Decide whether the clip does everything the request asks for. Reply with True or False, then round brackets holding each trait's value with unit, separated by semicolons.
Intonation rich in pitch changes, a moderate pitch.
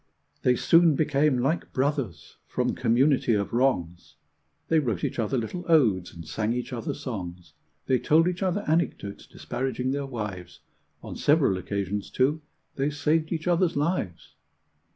False (6.9 semitones; 130 Hz)